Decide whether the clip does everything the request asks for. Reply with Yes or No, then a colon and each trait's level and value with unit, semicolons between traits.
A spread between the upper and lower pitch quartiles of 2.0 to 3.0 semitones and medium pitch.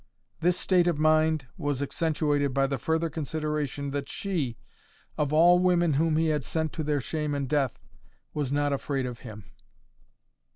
Yes: narrow, 2.4 semitones; medium, 150 Hz